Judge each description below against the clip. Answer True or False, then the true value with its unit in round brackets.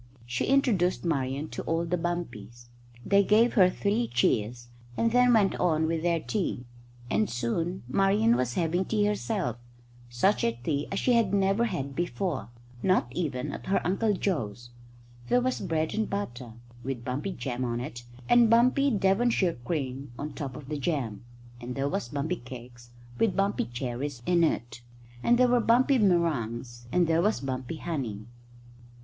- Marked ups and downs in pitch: True (8.0 semitones)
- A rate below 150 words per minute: False (165 wpm)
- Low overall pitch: False (165 Hz)